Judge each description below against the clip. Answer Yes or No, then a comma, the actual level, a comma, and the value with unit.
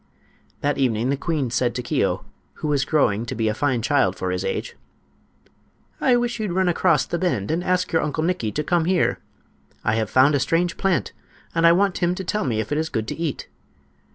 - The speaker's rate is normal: No, fast, 215 wpm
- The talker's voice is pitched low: No, medium, 150 Hz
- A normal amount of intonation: No, wide, 6.4 semitones